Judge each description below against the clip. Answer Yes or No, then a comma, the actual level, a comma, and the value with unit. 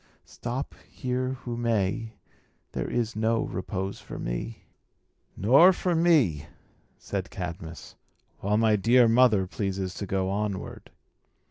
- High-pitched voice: No, low, 110 Hz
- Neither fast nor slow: No, slow, 120 wpm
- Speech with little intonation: No, average, 4.2 semitones